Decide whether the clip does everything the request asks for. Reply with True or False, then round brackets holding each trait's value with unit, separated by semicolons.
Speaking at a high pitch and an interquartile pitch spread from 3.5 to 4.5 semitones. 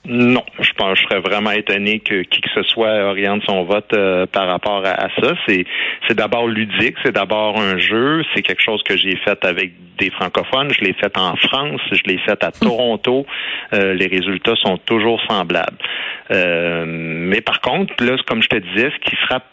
False (105 Hz; 4.1 semitones)